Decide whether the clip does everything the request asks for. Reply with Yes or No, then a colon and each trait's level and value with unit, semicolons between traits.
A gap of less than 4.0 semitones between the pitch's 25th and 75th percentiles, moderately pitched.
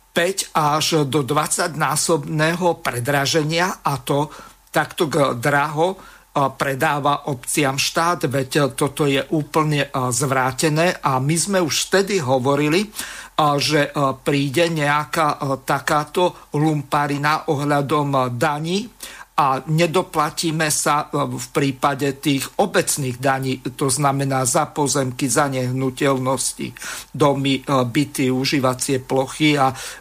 Yes: narrow, 2.6 semitones; medium, 145 Hz